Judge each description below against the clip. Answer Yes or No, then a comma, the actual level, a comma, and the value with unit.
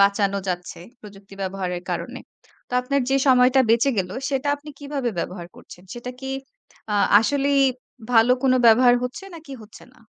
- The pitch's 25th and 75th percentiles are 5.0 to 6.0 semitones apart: Yes, wide, 5.5 semitones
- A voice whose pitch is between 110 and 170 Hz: No, high, 245 Hz